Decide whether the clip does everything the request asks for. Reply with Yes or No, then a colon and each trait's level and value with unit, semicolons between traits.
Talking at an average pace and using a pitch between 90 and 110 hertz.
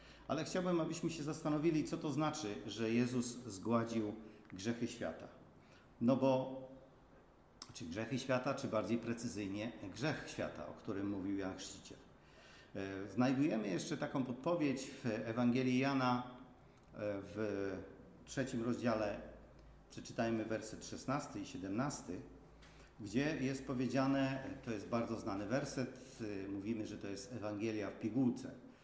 No: average, 120 wpm; low, 120 Hz